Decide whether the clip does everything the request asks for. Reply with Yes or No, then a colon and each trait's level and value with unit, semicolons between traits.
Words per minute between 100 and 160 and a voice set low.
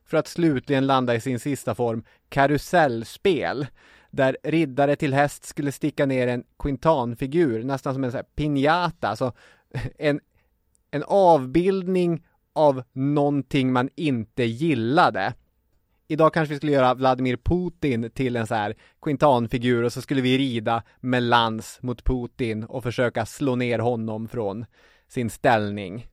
Yes: average, 140 wpm; low, 130 Hz